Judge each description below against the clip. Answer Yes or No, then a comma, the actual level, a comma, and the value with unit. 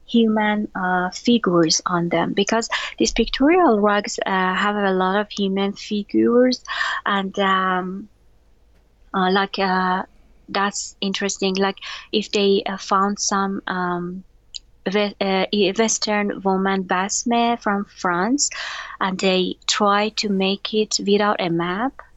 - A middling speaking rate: No, slow, 120 wpm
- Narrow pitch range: Yes, narrow, 2.3 semitones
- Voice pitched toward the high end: Yes, high, 200 Hz